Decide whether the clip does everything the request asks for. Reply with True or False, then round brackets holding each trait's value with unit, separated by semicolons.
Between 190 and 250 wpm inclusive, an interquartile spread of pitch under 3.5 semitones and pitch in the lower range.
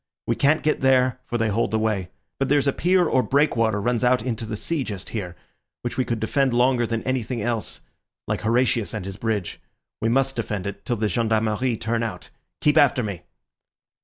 True (200 wpm; 3.1 semitones; 115 Hz)